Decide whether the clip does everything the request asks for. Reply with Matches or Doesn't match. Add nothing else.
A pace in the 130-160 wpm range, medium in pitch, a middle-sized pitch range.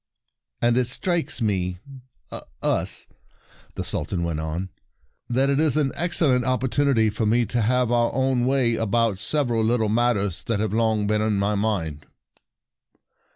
Doesn't match